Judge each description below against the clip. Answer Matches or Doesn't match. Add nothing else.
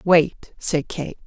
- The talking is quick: Doesn't match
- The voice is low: Doesn't match